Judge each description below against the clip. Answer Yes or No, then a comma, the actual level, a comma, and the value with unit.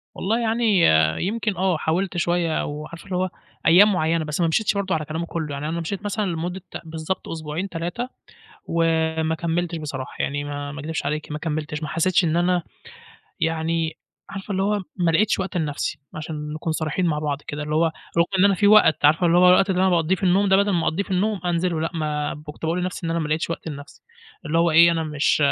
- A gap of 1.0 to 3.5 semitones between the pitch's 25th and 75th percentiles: Yes, average, 3.0 semitones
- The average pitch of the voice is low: No, medium, 165 Hz